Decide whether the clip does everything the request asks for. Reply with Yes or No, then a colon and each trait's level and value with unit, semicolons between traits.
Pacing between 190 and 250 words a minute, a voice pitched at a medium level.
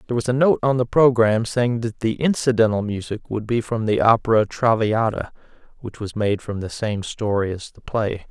No: average, 200 wpm; low, 110 Hz